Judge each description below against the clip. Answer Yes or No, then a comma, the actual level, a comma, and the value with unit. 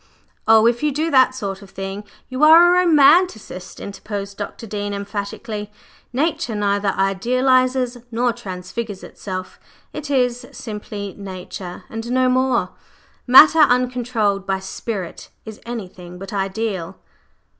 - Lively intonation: No, average, 4.4 semitones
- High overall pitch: Yes, high, 220 Hz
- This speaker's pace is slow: Yes, slow, 125 wpm